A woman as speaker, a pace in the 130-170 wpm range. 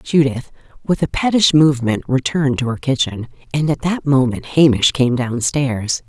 Yes: female; average, 160 wpm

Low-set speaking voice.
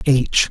Yes: low, 130 Hz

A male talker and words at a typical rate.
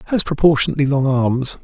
Yes: male; average, 145 wpm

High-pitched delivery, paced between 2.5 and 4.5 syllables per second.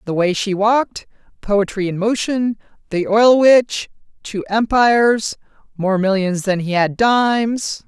Yes: high, 210 Hz; 4.0 syllables/s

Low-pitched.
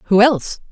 No: high, 220 Hz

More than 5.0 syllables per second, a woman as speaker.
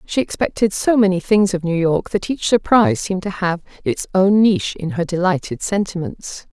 Yes: 5.3 syllables/s; female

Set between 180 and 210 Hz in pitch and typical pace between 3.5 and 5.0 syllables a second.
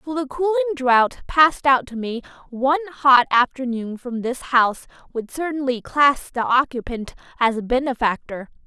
No: very high, 260 Hz; 4.7 syllables/s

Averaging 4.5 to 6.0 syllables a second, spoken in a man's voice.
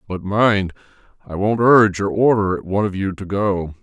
Yes: 5.0 syllables/s; male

